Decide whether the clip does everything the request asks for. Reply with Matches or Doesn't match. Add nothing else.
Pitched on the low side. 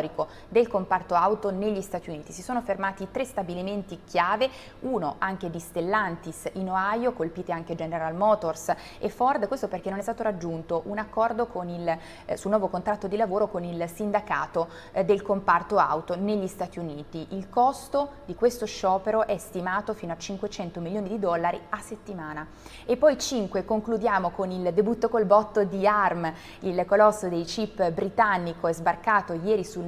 Doesn't match